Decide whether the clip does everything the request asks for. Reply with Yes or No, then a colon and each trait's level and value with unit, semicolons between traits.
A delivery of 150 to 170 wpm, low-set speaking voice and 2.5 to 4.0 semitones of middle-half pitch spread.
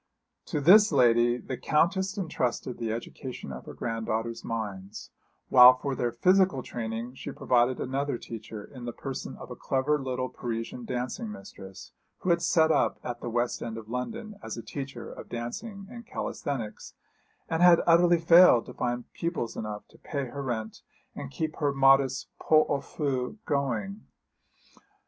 No: average, 165 wpm; low, 125 Hz; average, 4.8 semitones